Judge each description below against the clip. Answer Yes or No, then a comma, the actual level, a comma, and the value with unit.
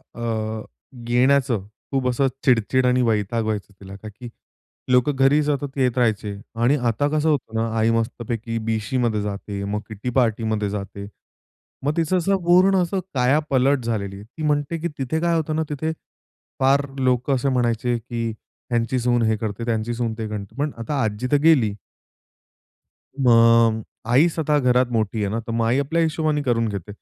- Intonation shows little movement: No, average, 4.2 semitones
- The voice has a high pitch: No, low, 120 Hz